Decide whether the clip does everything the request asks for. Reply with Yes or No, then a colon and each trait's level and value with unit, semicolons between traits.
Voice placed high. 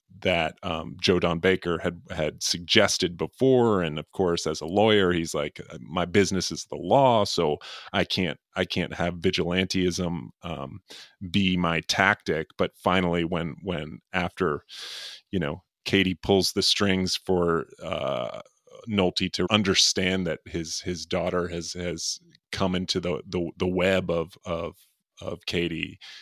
No: very low, 90 Hz